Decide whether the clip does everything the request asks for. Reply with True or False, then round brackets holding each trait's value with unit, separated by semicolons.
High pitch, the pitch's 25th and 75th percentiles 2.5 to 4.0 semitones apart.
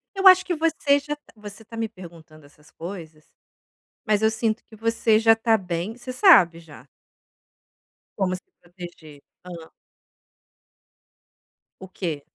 False (205 Hz; 5.1 semitones)